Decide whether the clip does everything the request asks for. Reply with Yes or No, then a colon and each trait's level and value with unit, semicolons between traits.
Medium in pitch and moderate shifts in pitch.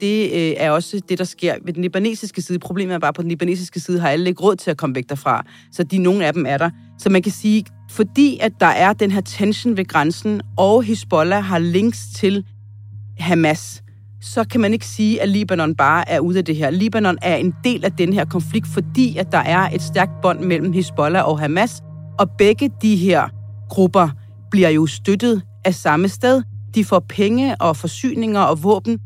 Yes: medium, 180 Hz; average, 4.6 semitones